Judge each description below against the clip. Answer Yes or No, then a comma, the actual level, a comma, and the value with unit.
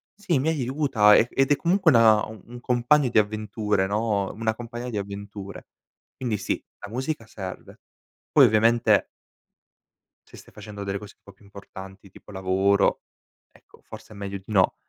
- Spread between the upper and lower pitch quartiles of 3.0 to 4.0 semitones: Yes, average, 3.3 semitones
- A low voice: Yes, low, 110 Hz